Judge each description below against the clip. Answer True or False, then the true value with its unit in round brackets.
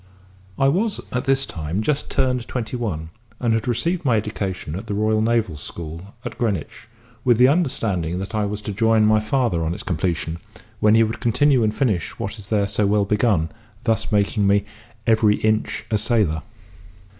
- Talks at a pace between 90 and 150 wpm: False (185 wpm)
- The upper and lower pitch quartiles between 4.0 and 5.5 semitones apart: False (3.2 semitones)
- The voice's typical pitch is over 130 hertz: False (110 Hz)